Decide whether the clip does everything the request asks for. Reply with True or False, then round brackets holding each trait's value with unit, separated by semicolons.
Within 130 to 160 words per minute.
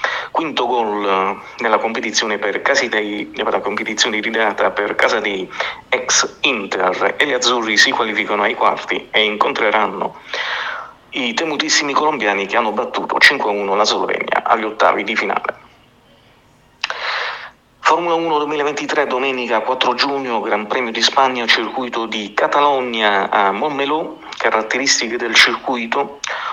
False (120 wpm)